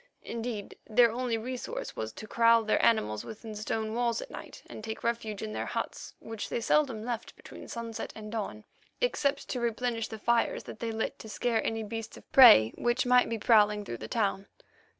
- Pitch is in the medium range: No, high, 225 Hz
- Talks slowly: No, average, 195 wpm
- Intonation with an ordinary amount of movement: No, narrow, 1.8 semitones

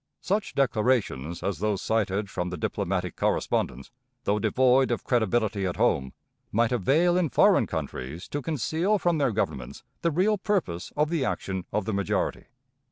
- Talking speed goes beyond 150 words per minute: Yes, average, 160 wpm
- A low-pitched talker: Yes, low, 110 Hz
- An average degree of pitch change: No, wide, 7.9 semitones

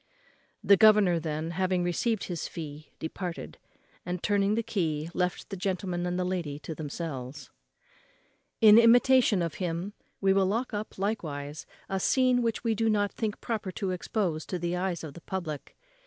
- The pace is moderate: Yes, average, 170 wpm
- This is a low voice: No, medium, 185 Hz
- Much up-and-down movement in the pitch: No, average, 4.1 semitones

